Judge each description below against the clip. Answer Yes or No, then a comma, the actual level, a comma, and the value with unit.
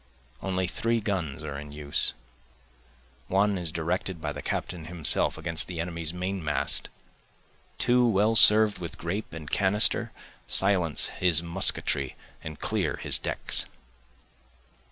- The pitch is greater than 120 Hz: No, very low, 90 Hz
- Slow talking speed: Yes, slow, 130 wpm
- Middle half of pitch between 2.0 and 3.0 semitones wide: No, average, 3.8 semitones